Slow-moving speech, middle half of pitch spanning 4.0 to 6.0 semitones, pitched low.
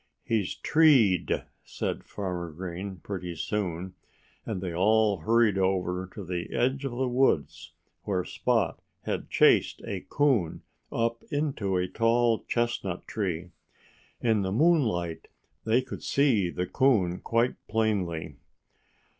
Yes: slow, 125 wpm; average, 4.7 semitones; low, 100 Hz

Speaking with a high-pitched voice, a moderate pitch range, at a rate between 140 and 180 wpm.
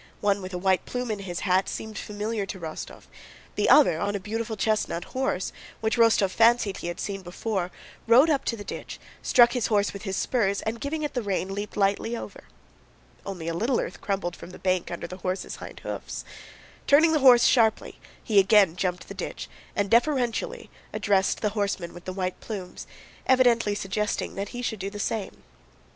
No: high, 205 Hz; average, 3.5 semitones; average, 195 wpm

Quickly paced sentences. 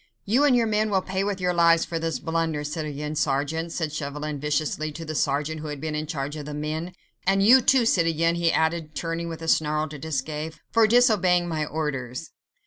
Yes: fast, 210 wpm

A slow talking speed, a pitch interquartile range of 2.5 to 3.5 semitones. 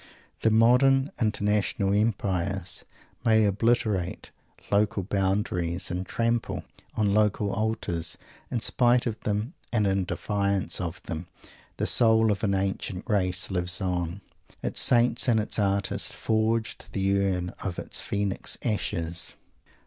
Yes: slow, 125 wpm; average, 2.9 semitones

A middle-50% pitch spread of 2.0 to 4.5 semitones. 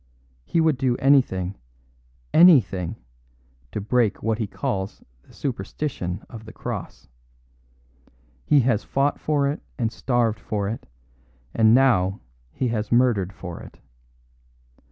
No: average, 5.0 semitones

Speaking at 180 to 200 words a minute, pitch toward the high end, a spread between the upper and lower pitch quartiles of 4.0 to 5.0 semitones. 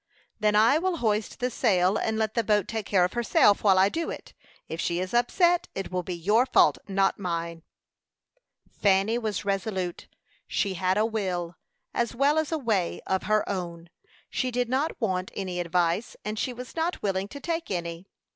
Yes: average, 190 wpm; high, 205 Hz; average, 4.5 semitones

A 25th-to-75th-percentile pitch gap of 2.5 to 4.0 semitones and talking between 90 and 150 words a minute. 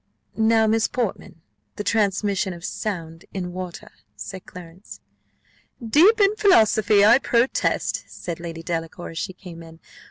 No: average, 4.7 semitones; slow, 135 wpm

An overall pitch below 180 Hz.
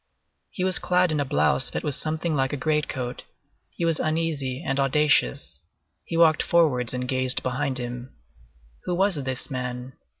Yes: medium, 140 Hz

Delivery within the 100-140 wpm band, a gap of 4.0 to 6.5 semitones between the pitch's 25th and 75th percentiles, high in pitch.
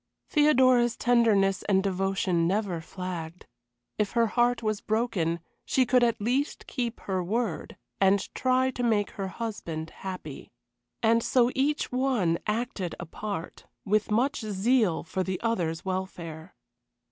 Yes: slow, 135 wpm; average, 4.6 semitones; high, 210 Hz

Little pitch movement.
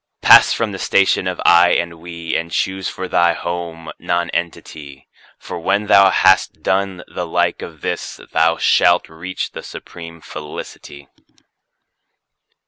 Yes: narrow, 2.1 semitones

